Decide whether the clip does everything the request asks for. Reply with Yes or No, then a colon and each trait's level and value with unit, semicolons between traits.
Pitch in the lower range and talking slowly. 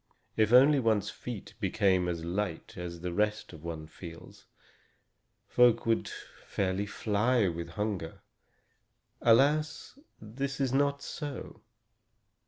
Yes: low, 105 Hz; slow, 115 wpm